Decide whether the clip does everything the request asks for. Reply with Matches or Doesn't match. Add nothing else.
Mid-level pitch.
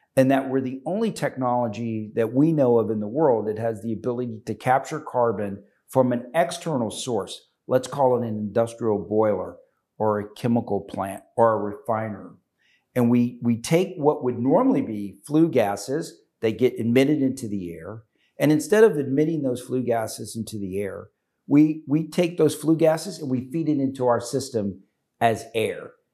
Doesn't match